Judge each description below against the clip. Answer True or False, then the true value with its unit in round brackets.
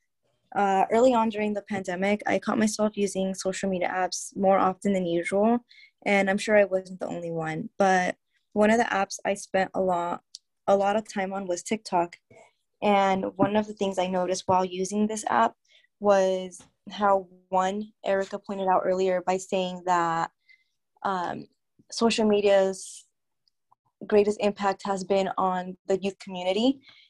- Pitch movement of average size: False (2.0 semitones)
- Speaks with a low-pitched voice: False (195 Hz)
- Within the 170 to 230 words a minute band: False (160 wpm)